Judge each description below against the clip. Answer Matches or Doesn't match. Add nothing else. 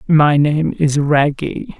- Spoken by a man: Doesn't match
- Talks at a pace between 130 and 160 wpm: Matches